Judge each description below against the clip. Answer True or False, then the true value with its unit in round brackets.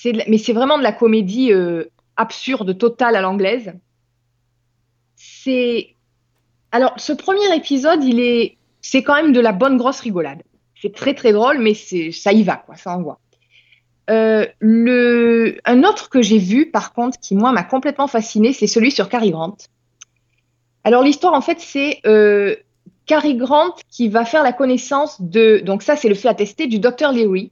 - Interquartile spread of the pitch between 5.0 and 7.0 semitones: True (5.5 semitones)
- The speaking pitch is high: True (225 Hz)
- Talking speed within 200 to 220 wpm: False (175 wpm)